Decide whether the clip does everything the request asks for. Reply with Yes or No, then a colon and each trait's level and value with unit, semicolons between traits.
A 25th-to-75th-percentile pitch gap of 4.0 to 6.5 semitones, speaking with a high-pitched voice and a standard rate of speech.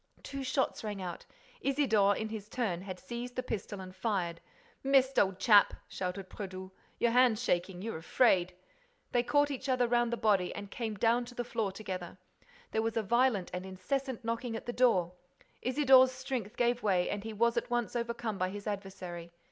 Yes: average, 4.3 semitones; high, 220 Hz; average, 190 wpm